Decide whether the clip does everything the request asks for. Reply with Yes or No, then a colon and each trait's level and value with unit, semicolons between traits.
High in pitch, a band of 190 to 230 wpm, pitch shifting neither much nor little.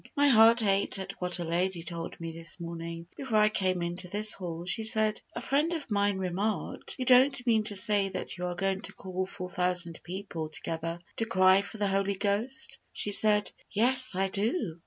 Yes: high, 195 Hz; average, 200 wpm; average, 3.4 semitones